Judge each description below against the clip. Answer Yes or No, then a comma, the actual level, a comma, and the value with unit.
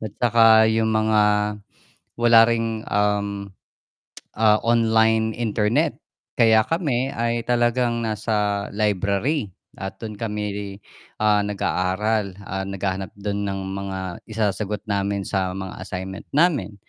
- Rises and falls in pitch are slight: Yes, narrow, 2.2 semitones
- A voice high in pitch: No, low, 105 Hz